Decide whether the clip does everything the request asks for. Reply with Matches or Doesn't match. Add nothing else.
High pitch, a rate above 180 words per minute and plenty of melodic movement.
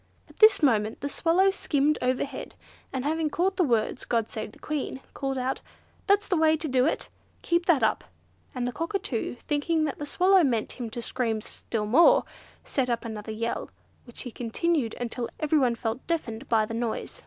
Matches